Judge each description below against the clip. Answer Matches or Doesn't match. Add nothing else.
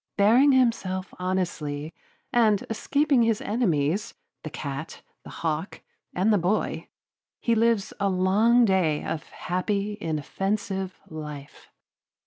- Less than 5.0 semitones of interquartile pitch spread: Doesn't match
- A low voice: Doesn't match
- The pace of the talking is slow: Matches